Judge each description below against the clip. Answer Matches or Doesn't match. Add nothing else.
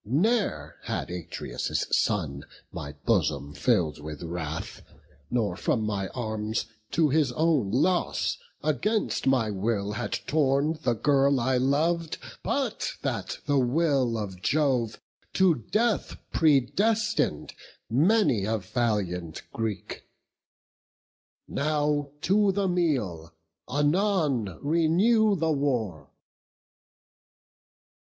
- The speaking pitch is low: Matches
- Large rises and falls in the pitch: Matches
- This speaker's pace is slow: Matches